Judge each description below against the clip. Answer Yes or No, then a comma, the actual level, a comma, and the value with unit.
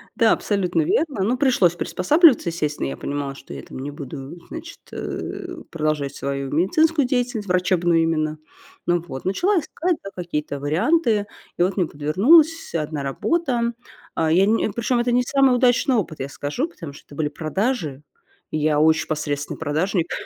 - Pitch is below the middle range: No, medium, 175 Hz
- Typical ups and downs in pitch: No, wide, 8.5 semitones